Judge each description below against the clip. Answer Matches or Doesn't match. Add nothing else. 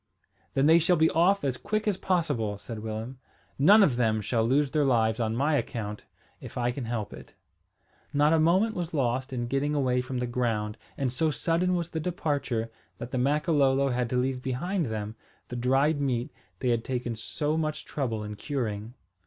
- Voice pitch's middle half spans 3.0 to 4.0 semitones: Doesn't match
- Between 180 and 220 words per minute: Matches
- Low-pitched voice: Matches